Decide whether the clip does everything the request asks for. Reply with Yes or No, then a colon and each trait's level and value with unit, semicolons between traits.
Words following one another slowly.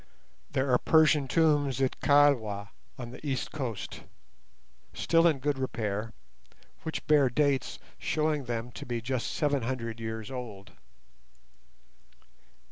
Yes: slow, 125 wpm